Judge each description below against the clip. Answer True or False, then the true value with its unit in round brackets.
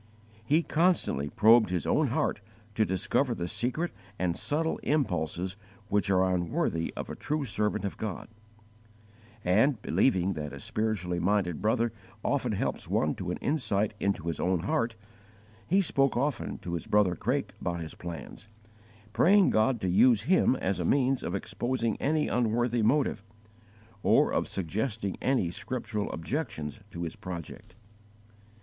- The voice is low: True (105 Hz)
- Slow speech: False (150 wpm)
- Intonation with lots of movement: True (6.2 semitones)